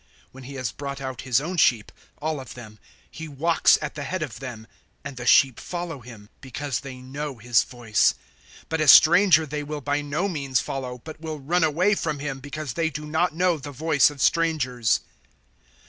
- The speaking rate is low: No, fast, 205 wpm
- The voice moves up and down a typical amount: Yes, average, 3.5 semitones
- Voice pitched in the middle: Yes, medium, 145 Hz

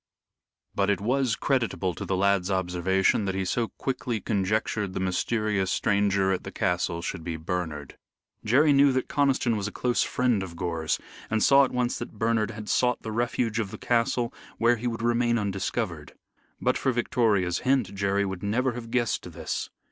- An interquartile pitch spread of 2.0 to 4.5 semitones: Yes, average, 4.1 semitones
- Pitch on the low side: Yes, low, 105 Hz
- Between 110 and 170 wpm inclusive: No, average, 180 wpm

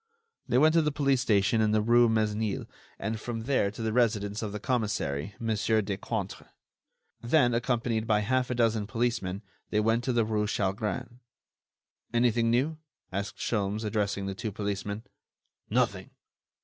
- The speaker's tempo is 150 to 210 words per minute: Yes, average, 155 wpm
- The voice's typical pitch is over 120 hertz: No, low, 110 Hz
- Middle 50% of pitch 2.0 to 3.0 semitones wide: Yes, narrow, 2.5 semitones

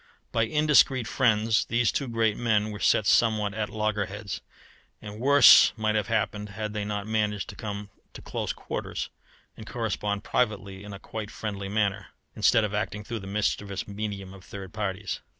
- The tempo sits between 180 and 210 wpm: No, average, 170 wpm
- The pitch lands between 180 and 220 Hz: No, low, 105 Hz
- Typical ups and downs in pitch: No, narrow, 1.5 semitones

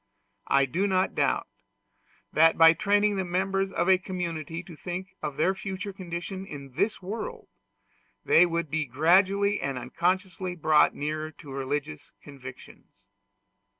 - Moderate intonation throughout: Yes, average, 4.0 semitones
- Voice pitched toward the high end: No, medium, 175 Hz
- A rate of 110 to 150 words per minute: Yes, average, 140 wpm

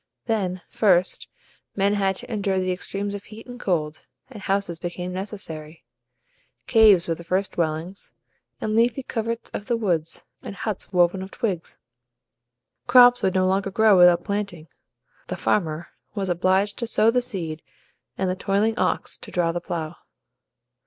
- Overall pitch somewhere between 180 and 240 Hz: Yes, high, 190 Hz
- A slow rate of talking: No, average, 160 wpm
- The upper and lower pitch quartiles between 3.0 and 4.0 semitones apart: Yes, average, 3.4 semitones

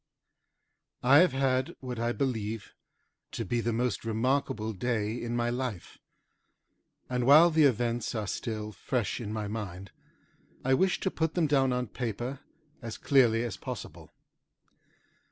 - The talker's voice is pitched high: No, low, 120 Hz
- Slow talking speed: No, average, 145 wpm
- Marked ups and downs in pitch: No, average, 3.1 semitones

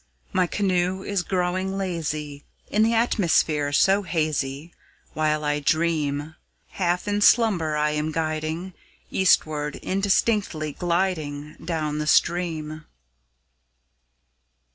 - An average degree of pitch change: Yes, average, 3.7 semitones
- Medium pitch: Yes, medium, 165 Hz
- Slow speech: Yes, slow, 100 wpm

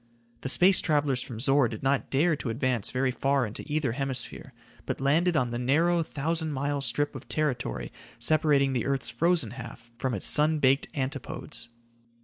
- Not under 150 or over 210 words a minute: Yes, average, 170 wpm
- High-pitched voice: No, low, 135 Hz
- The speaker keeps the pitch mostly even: No, average, 3.3 semitones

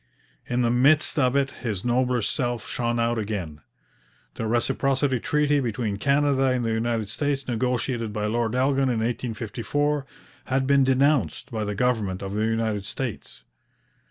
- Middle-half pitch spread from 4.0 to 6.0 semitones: No, average, 3.3 semitones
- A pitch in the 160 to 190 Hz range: No, low, 120 Hz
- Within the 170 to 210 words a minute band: No, average, 155 wpm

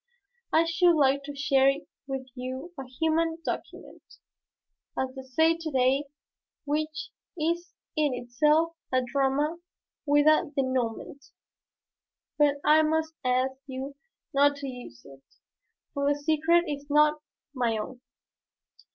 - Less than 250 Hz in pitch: No, very high, 285 Hz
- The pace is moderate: No, slow, 125 wpm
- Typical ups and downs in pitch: Yes, average, 3.0 semitones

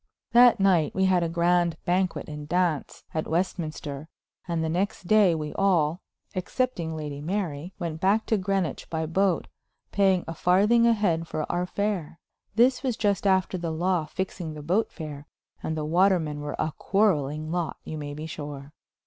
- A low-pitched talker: No, medium, 175 Hz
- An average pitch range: Yes, average, 3.7 semitones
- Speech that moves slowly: No, average, 175 wpm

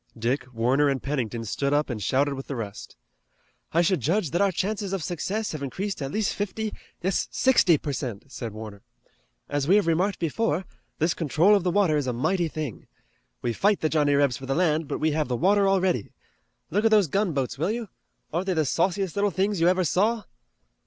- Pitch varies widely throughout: Yes, wide, 6.0 semitones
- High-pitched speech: No, medium, 160 Hz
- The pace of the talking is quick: Yes, fast, 210 wpm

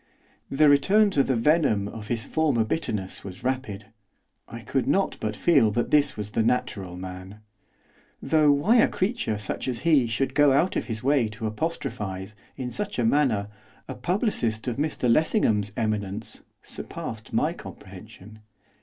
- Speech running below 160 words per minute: No, average, 165 wpm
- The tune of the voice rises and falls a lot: Yes, wide, 5.7 semitones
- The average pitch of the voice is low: Yes, low, 120 Hz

